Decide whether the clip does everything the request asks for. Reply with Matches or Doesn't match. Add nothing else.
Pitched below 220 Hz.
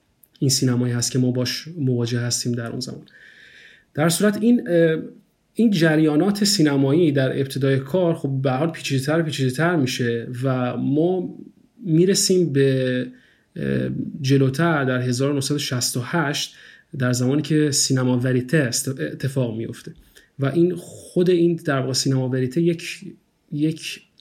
Matches